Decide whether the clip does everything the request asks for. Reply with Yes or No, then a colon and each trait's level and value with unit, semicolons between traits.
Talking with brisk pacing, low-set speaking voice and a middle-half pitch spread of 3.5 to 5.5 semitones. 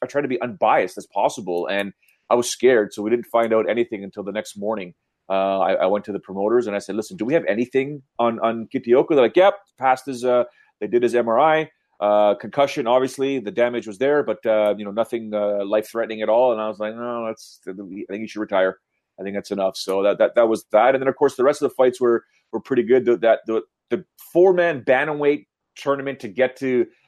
Yes: fast, 245 wpm; low, 120 Hz; average, 3.8 semitones